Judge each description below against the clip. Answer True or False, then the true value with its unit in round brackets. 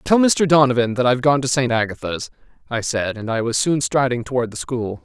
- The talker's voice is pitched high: False (125 Hz)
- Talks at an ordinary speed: False (225 wpm)